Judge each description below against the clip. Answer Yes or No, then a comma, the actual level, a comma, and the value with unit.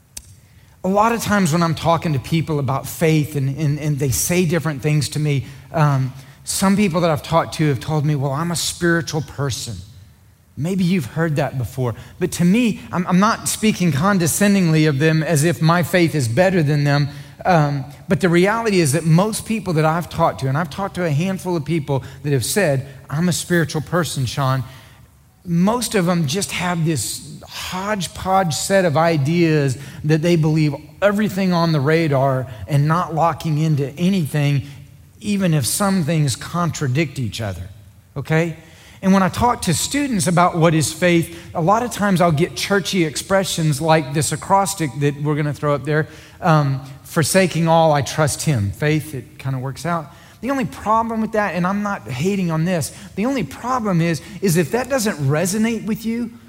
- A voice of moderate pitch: Yes, medium, 160 Hz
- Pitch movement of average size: Yes, average, 4.3 semitones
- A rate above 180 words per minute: Yes, average, 190 wpm